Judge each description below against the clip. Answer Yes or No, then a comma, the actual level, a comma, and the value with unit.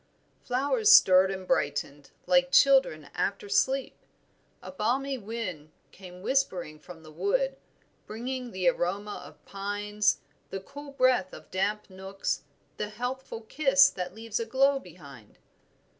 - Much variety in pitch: Yes, wide, 6.3 semitones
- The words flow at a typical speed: No, slow, 130 wpm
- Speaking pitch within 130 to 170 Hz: No, high, 210 Hz